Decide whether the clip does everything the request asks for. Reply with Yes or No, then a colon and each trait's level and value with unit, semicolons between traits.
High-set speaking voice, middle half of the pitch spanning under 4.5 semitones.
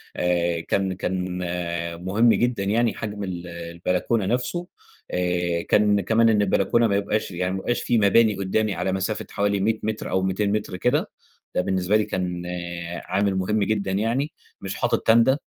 No: low, 100 Hz; average, 3.0 semitones